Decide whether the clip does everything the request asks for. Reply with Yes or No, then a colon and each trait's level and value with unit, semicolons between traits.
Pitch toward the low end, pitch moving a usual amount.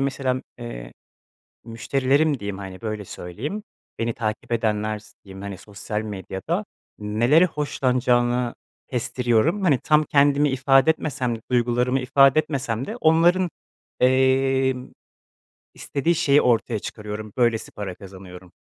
Yes: low, 125 Hz; average, 4.4 semitones